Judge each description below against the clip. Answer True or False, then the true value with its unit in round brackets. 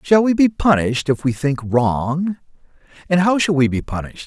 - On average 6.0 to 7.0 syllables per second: False (5.2 syllables/s)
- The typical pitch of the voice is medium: True (155 Hz)